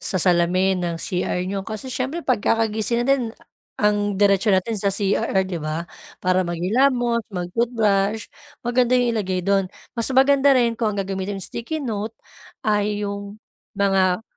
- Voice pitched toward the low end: No, high, 205 Hz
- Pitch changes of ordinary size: Yes, average, 3.7 semitones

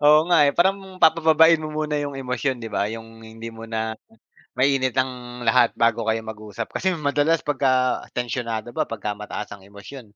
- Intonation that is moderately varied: Yes, average, 4.8 semitones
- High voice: No, low, 125 Hz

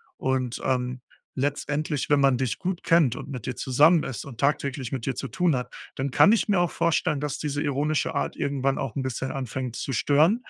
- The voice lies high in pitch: No, medium, 140 Hz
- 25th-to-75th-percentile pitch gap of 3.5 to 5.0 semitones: No, average, 2.7 semitones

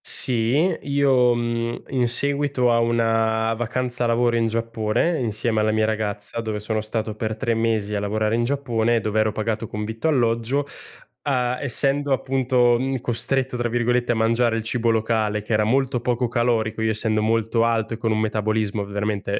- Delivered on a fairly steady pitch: Yes, narrow, 2.0 semitones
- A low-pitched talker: Yes, low, 115 Hz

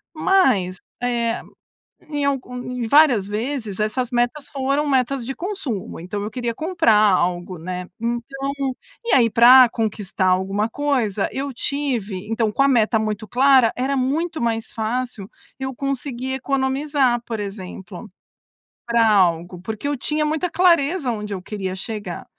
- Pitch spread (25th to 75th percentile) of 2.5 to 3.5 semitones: No, average, 4.7 semitones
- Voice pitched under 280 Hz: Yes, high, 240 Hz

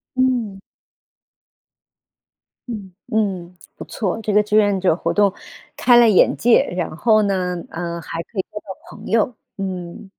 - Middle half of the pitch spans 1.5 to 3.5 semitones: Yes, average, 3.1 semitones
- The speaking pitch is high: Yes, high, 200 Hz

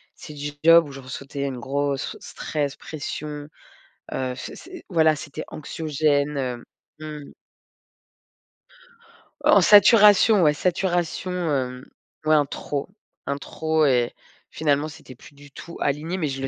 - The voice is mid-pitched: Yes, medium, 150 Hz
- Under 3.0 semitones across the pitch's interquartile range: Yes, narrow, 2.6 semitones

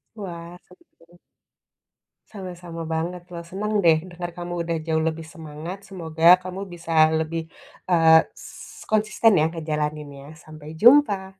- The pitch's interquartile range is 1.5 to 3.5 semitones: Yes, narrow, 2.4 semitones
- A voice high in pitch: No, medium, 170 Hz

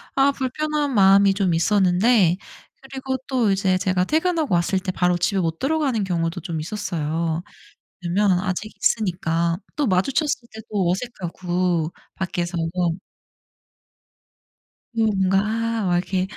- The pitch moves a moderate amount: Yes, average, 4.5 semitones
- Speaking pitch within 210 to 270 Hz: No, high, 190 Hz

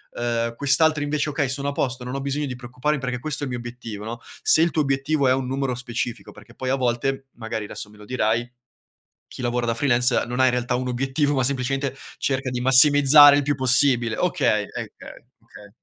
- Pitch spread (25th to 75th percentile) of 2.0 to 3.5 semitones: Yes, narrow, 2.5 semitones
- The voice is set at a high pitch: No, low, 130 Hz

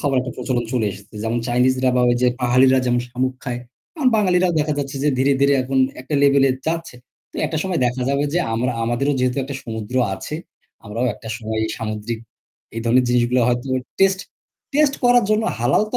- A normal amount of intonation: Yes, average, 3.0 semitones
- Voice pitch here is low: Yes, low, 130 Hz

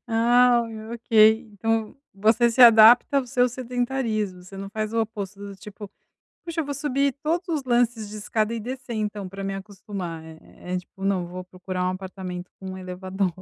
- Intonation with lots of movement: No, average, 4.2 semitones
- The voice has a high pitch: Yes, high, 215 Hz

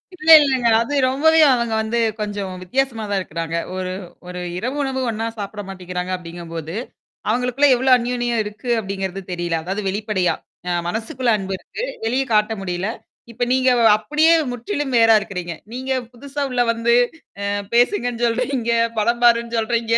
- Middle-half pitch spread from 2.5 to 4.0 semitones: No, average, 4.5 semitones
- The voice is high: Yes, high, 230 Hz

